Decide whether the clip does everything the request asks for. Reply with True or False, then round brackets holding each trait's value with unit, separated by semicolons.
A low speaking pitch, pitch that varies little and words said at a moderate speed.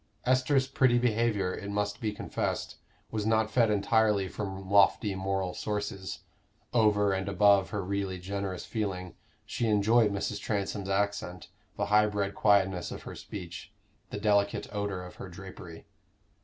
True (100 Hz; 1.8 semitones; 145 wpm)